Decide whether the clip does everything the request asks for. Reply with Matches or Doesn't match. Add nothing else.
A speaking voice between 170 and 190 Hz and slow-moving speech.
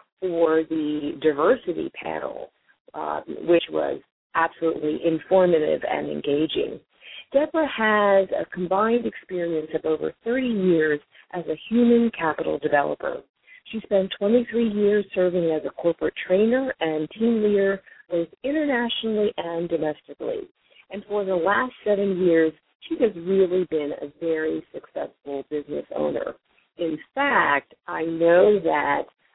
Matches